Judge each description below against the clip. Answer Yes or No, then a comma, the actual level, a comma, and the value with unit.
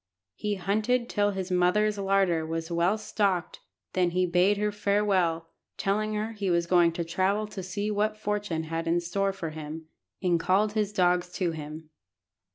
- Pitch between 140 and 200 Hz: Yes, medium, 185 Hz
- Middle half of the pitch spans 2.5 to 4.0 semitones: Yes, average, 3.3 semitones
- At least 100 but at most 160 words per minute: No, average, 170 wpm